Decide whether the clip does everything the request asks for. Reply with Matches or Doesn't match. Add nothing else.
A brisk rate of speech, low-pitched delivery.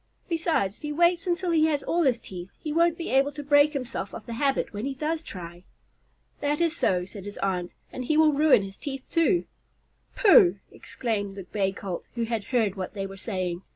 Doesn't match